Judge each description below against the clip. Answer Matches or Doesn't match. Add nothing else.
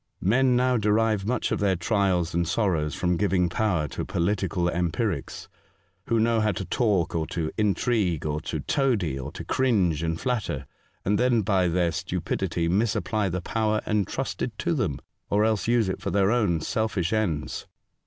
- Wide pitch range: Doesn't match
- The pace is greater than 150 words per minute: Matches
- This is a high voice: Doesn't match